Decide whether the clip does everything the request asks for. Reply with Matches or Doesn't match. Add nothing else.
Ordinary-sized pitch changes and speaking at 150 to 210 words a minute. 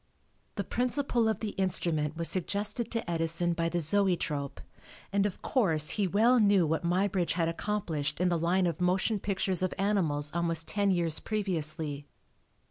Matches